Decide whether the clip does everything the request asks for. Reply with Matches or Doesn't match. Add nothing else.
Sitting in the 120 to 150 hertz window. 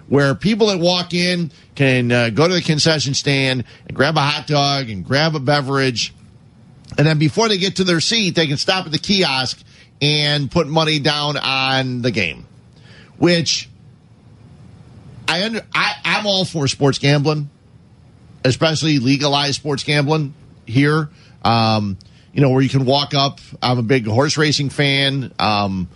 Matches